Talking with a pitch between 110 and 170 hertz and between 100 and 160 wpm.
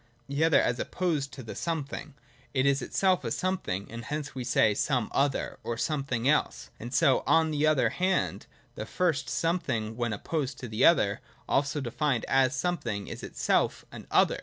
No: medium, 140 Hz; average, 175 wpm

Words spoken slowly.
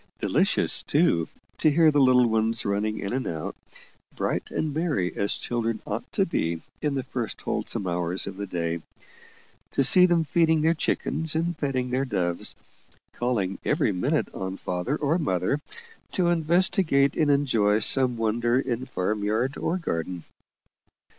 No: average, 155 wpm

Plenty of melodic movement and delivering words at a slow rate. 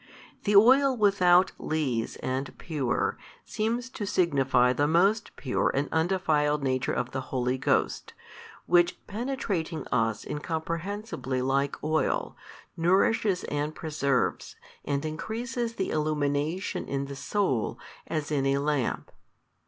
Yes: wide, 5.9 semitones; slow, 120 wpm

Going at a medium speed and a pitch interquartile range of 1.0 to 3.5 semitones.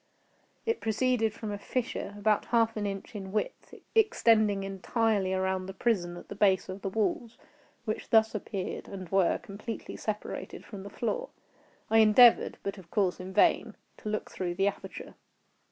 Yes: average, 170 wpm; average, 2.7 semitones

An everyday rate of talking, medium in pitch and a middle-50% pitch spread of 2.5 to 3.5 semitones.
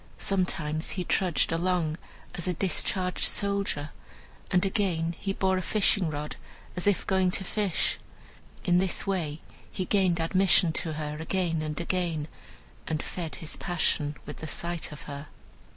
Yes: average, 150 wpm; medium, 175 Hz; average, 3.1 semitones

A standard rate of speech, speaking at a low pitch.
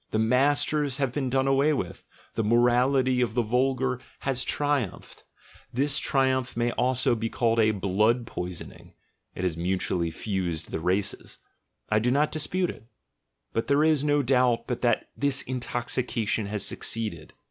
Yes: average, 160 wpm; low, 125 Hz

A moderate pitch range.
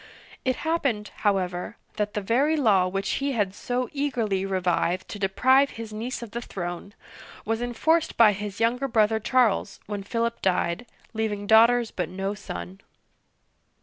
Yes: average, 3.8 semitones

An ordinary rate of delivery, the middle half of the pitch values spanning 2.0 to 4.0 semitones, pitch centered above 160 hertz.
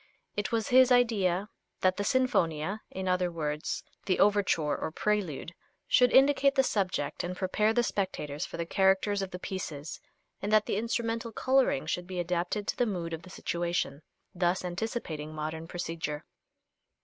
No: average, 160 wpm; average, 4.4 semitones; medium, 185 Hz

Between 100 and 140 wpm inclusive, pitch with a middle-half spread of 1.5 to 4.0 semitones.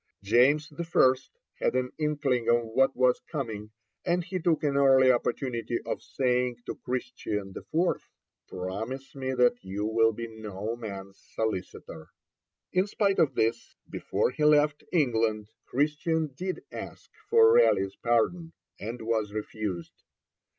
No: slow, 135 wpm; average, 5.3 semitones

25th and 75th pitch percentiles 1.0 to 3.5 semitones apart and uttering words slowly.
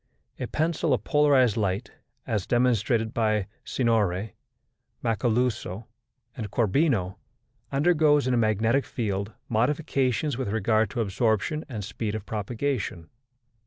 No: average, 3.9 semitones; slow, 115 wpm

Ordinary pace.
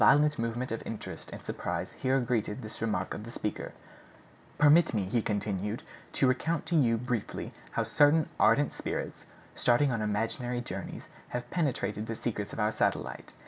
Yes: average, 170 wpm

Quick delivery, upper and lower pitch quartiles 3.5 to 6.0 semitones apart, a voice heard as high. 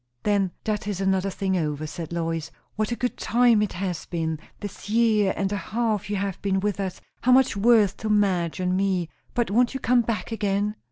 No: fast, 210 wpm; average, 2.8 semitones; high, 200 Hz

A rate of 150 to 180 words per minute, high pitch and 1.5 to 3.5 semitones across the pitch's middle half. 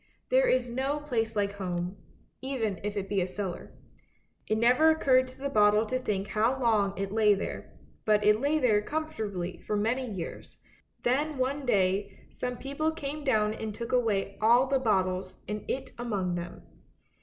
No: average, 175 wpm; high, 220 Hz; average, 4.5 semitones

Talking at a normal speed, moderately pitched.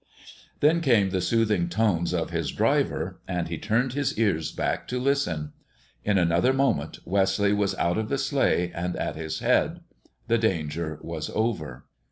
No: average, 165 wpm; very low, 95 Hz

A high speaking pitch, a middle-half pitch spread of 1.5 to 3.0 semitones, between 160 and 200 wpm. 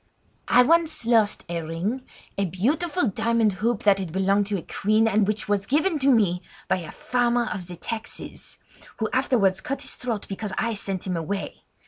No: high, 215 Hz; average, 4.1 semitones; average, 180 wpm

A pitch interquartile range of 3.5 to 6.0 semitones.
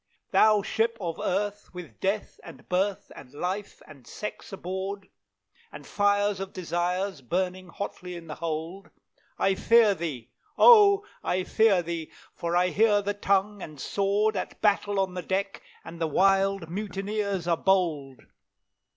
No: average, 2.9 semitones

